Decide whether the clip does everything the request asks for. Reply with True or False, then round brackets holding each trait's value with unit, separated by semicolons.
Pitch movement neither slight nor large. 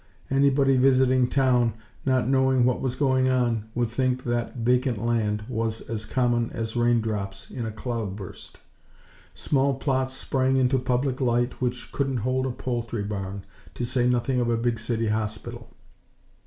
False (2.3 semitones)